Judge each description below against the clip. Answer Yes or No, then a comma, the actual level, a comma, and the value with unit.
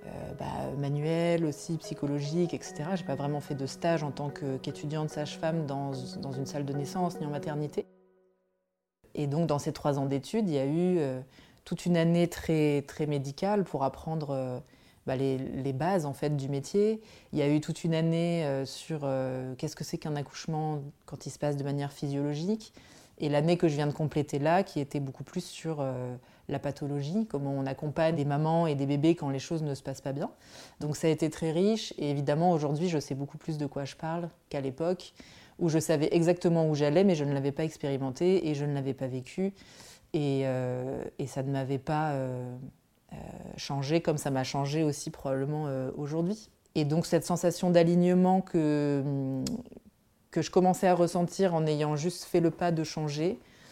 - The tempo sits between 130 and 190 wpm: No, average, 205 wpm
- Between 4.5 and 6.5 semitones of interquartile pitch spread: No, average, 3.3 semitones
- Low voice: No, medium, 150 Hz